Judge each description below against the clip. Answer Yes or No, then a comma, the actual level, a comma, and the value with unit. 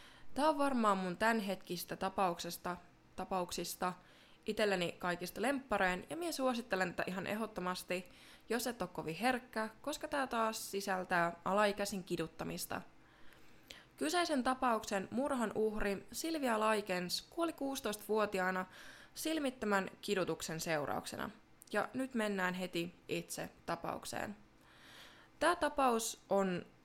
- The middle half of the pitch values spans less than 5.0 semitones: No, wide, 5.5 semitones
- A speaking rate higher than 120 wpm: No, average, 105 wpm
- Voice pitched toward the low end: No, high, 205 Hz